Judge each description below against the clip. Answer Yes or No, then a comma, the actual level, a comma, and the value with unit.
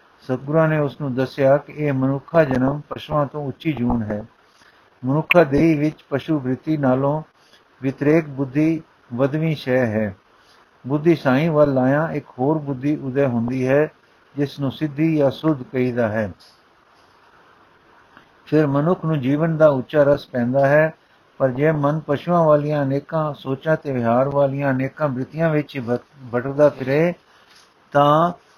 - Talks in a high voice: No, medium, 140 Hz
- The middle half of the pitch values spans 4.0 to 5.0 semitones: No, average, 2.8 semitones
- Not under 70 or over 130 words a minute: No, average, 140 wpm